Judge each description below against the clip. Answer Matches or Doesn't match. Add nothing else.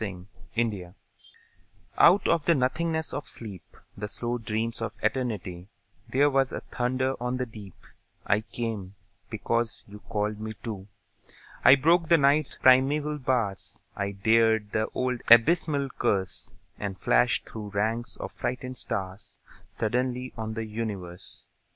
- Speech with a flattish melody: Doesn't match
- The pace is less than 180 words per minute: Matches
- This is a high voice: Doesn't match